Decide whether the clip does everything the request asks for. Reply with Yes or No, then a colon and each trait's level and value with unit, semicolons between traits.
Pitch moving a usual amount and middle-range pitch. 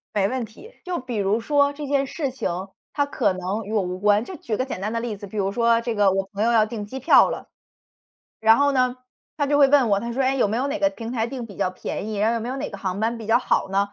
No: average, 4.5 semitones; high, 230 Hz